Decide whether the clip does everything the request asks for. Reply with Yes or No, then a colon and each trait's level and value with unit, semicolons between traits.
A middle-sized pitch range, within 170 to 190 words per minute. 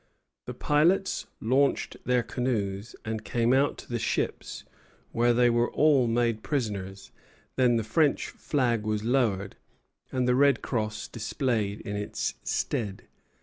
No: average, 3.3 semitones; average, 140 wpm